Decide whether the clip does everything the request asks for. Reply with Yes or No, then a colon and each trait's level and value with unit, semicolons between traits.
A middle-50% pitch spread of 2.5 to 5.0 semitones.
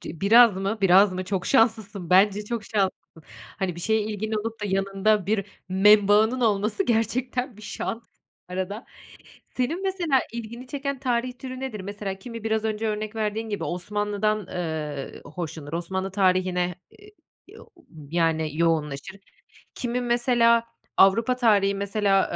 Yes: average, 3.5 semitones